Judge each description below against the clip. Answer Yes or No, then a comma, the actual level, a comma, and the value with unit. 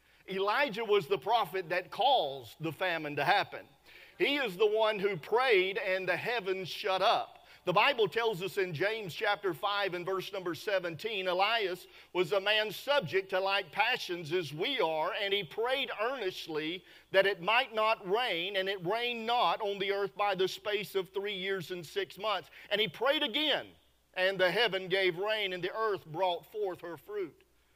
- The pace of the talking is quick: No, average, 185 wpm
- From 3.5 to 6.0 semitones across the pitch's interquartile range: No, average, 2.9 semitones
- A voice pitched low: No, high, 195 Hz